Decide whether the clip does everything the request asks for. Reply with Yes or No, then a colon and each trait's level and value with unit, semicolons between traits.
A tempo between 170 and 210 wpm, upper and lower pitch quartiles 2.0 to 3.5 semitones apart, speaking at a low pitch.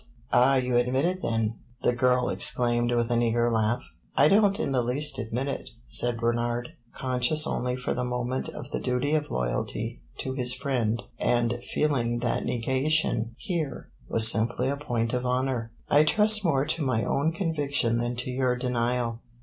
Yes: average, 175 wpm; average, 2.7 semitones; low, 125 Hz